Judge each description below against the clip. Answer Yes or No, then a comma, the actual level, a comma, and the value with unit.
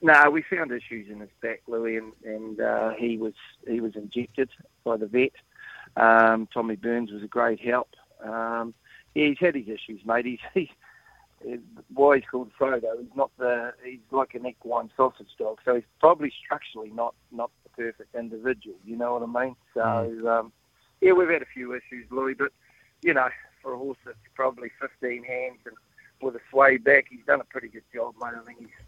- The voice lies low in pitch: Yes, low, 120 Hz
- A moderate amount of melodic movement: No, narrow, 2.3 semitones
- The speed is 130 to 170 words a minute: No, average, 200 wpm